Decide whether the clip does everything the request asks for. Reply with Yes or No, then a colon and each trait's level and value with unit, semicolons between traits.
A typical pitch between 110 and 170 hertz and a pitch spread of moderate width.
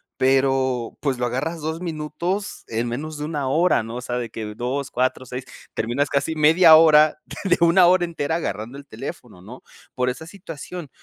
Yes: medium, 140 Hz; average, 4.5 semitones